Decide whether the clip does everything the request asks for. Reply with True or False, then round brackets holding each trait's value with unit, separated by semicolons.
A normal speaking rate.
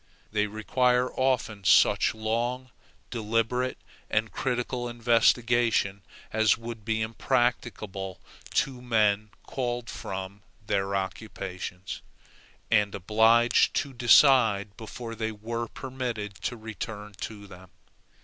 False (100 wpm)